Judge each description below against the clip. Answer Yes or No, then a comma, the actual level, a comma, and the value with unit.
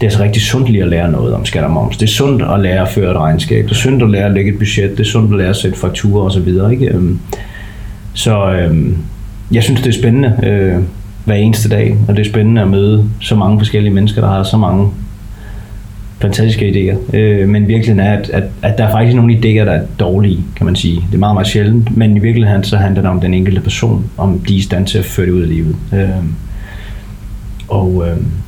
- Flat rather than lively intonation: Yes, narrow, 2.0 semitones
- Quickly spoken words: Yes, fast, 250 wpm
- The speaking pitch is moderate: No, low, 100 Hz